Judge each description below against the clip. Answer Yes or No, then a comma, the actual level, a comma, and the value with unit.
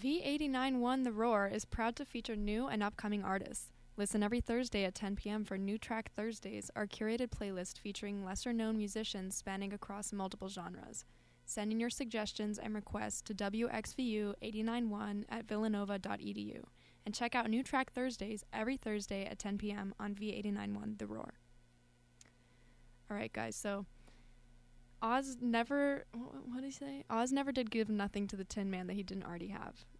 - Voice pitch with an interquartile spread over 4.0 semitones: No, average, 3.1 semitones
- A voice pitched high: Yes, high, 210 Hz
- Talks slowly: No, average, 160 wpm